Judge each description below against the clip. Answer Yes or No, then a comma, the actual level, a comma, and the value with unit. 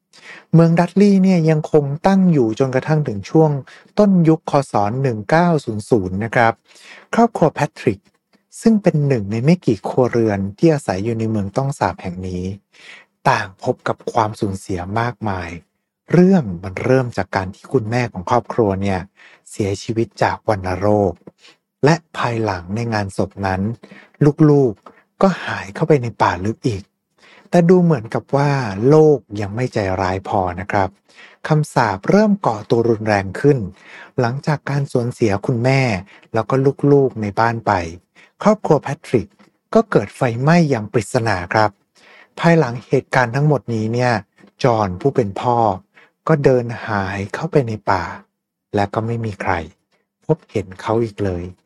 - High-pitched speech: No, low, 120 Hz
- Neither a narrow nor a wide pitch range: No, wide, 6.6 semitones